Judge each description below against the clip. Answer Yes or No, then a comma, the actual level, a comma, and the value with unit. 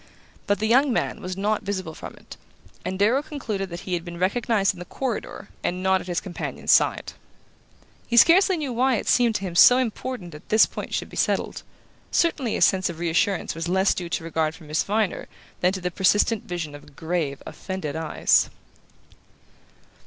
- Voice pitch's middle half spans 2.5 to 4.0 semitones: No, average, 4.7 semitones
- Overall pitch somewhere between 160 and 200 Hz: Yes, high, 190 Hz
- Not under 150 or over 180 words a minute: No, average, 190 wpm